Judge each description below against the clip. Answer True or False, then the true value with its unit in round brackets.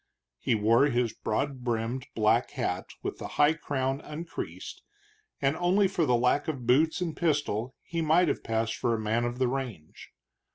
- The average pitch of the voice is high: False (130 Hz)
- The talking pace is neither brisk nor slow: True (175 wpm)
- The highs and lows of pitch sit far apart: False (4.8 semitones)